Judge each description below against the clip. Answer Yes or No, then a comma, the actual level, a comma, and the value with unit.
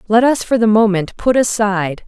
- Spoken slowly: No, average, 200 wpm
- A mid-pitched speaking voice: No, high, 215 Hz